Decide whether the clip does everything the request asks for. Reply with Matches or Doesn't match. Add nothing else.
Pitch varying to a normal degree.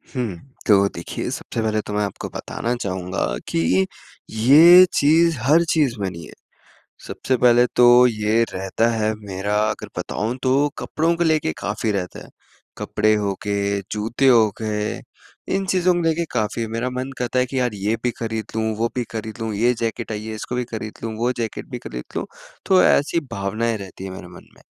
Matches